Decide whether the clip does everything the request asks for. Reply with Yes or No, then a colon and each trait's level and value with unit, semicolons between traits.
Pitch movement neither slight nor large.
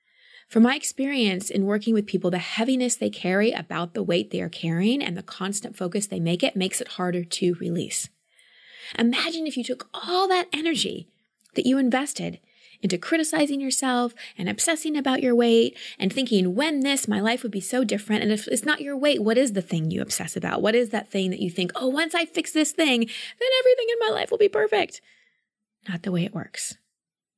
No: wide, 7.1 semitones